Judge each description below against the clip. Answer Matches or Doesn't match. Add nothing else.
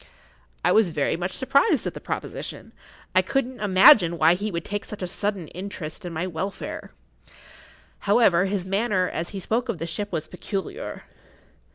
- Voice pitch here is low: Doesn't match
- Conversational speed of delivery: Matches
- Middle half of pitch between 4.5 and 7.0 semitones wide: Doesn't match